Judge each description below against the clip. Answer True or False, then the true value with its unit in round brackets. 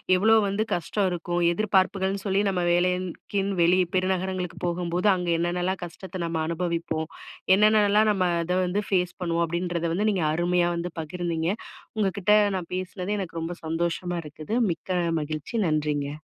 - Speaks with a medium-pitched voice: True (180 Hz)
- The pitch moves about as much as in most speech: False (2.0 semitones)